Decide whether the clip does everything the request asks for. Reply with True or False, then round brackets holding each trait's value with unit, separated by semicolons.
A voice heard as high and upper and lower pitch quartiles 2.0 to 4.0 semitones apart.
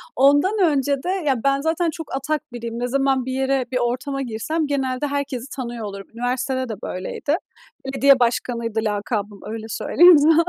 True (265 Hz; 3.2 semitones)